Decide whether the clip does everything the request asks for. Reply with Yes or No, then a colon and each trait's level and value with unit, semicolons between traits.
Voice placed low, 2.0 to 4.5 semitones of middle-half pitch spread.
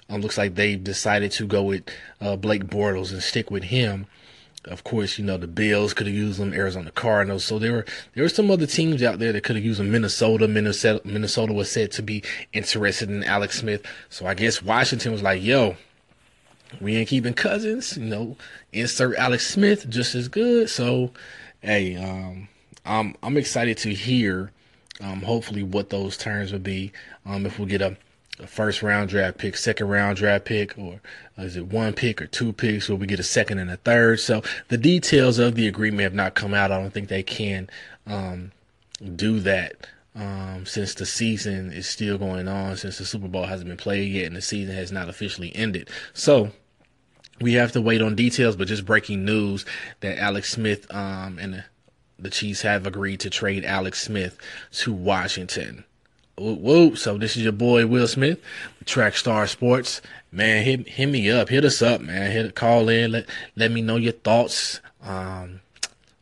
Yes: low, 105 Hz; average, 2.9 semitones